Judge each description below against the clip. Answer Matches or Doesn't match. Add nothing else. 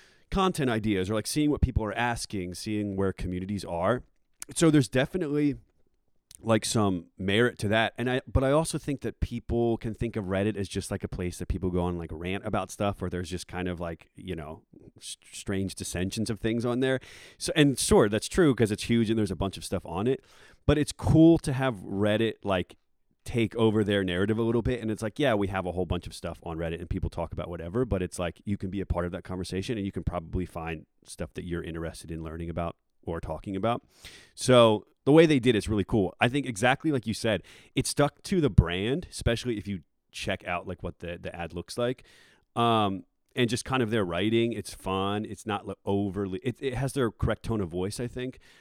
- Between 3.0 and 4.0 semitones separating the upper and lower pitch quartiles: Doesn't match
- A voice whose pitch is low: Matches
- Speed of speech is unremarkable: Doesn't match